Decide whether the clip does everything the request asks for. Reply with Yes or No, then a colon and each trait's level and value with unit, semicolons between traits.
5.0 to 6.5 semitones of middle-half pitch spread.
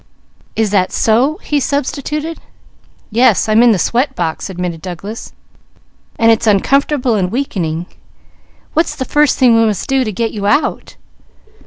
Yes: wide, 5.5 semitones